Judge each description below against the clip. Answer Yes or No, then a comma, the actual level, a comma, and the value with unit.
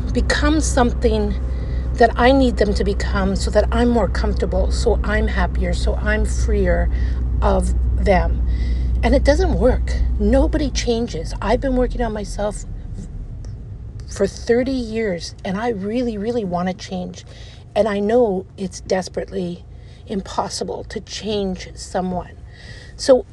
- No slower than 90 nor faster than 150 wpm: Yes, slow, 135 wpm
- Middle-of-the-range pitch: Yes, medium, 175 Hz